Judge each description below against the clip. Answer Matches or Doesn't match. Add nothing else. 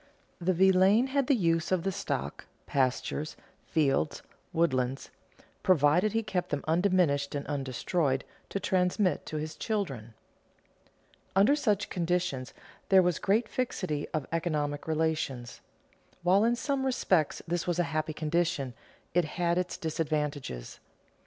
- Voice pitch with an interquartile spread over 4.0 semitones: Matches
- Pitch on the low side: Doesn't match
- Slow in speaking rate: Matches